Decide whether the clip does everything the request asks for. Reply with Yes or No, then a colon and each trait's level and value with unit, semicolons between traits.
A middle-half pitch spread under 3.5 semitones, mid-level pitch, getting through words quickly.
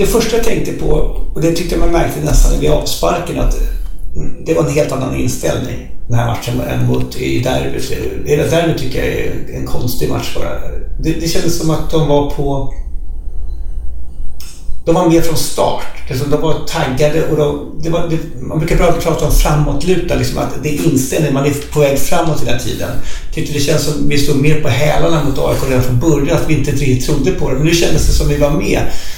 No: average, 4.4 semitones; medium, 145 Hz; fast, 210 wpm